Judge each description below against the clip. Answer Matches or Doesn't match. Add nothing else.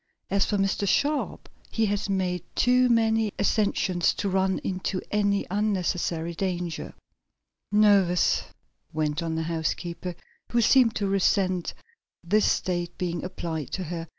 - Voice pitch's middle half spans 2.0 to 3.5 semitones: Matches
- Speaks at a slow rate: Matches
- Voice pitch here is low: Doesn't match